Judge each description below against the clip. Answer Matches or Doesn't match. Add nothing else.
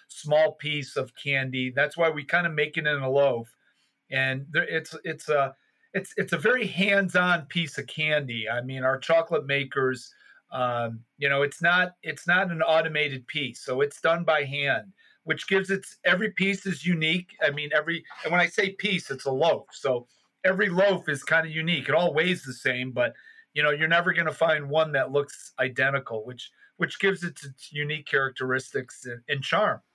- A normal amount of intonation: Matches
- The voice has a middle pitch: Matches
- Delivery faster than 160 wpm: Matches